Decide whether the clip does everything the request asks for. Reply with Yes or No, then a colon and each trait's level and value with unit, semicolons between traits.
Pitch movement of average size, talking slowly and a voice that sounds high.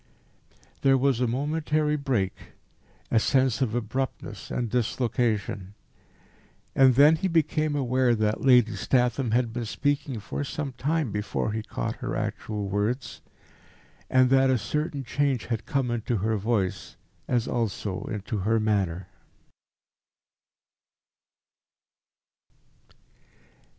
No: average, 3.9 semitones; slow, 115 wpm; low, 120 Hz